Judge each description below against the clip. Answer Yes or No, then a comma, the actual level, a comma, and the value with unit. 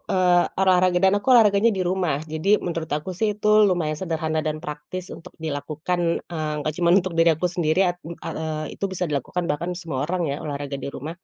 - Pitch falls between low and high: Yes, medium, 165 Hz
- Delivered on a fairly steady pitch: No, average, 3.1 semitones